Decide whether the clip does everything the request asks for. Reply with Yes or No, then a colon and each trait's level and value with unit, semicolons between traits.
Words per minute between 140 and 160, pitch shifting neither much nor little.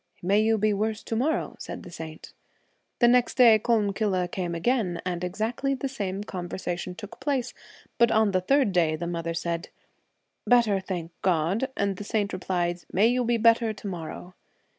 No: average, 180 wpm; average, 4.5 semitones